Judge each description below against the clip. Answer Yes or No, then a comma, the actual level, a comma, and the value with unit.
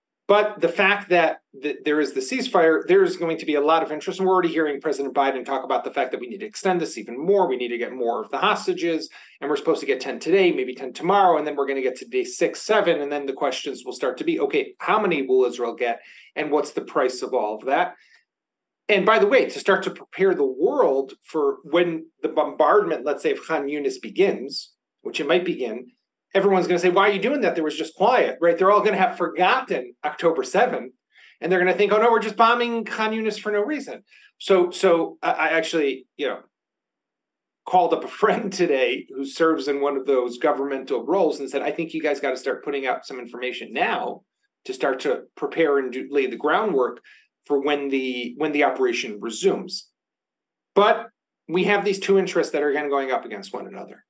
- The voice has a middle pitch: Yes, medium, 180 Hz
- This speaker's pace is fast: Yes, fast, 230 wpm